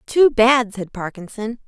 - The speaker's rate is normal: Yes, average, 145 wpm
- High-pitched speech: Yes, high, 225 Hz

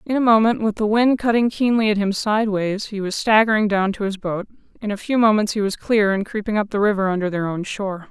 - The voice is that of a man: No, female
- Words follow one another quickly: Yes, fast, 250 wpm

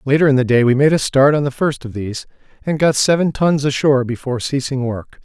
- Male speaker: Yes, male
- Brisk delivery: Yes, fast, 240 wpm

